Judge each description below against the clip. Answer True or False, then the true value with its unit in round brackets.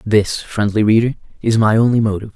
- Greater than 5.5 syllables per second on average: True (6.0 syllables/s)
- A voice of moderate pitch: False (110 Hz)